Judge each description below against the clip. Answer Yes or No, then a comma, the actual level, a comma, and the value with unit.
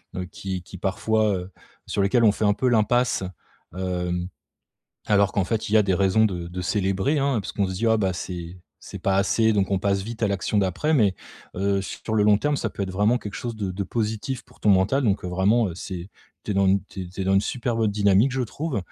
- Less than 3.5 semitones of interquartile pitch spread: Yes, average, 2.7 semitones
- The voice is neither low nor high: No, low, 100 Hz